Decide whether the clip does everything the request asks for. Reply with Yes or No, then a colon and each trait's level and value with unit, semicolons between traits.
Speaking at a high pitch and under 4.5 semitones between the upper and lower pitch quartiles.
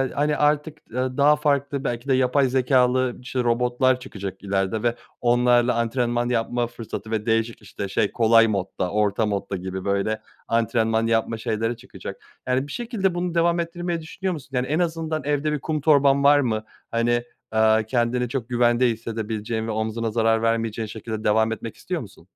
No: low, 120 Hz; average, 4.0 semitones